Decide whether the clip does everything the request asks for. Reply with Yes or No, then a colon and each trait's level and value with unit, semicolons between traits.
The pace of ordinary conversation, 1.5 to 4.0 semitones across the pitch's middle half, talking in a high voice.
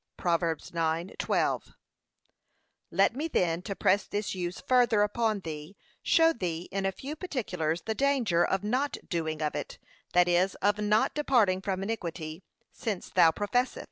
No: average, 150 wpm; average, 4.8 semitones; high, 195 Hz